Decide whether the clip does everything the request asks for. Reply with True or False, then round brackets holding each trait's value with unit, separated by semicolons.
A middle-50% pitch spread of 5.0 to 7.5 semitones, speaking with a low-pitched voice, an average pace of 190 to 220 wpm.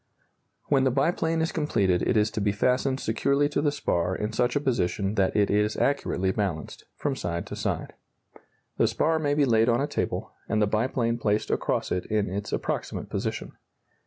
True (5.3 semitones; 115 Hz; 195 wpm)